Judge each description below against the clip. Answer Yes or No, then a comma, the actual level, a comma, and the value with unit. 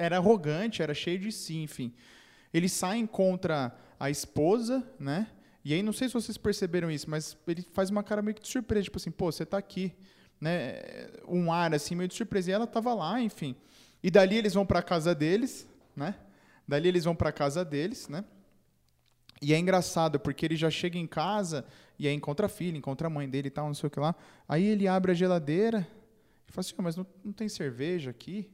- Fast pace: Yes, fast, 220 wpm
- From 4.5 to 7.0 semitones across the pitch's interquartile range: Yes, average, 5.2 semitones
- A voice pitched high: No, medium, 175 Hz